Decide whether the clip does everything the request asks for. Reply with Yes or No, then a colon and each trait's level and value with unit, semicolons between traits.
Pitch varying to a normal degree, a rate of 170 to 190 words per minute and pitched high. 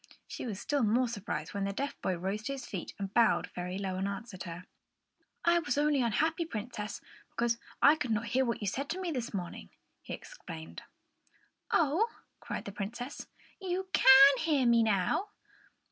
No: wide, 6.2 semitones; average, 180 wpm; high, 235 Hz